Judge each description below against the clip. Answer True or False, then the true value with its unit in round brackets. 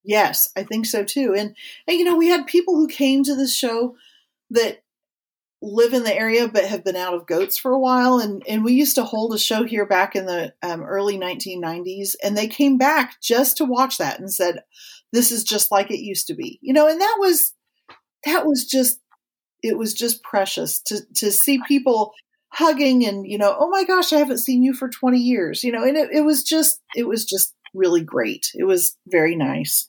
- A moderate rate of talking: False (220 wpm)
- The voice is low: False (245 Hz)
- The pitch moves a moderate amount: False (6.3 semitones)